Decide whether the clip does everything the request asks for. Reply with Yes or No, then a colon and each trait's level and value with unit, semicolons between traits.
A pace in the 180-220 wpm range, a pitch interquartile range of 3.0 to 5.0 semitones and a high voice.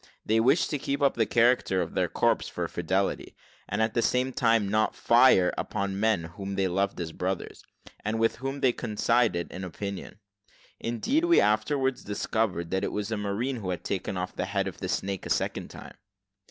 No: average, 195 wpm; average, 3.6 semitones; low, 105 Hz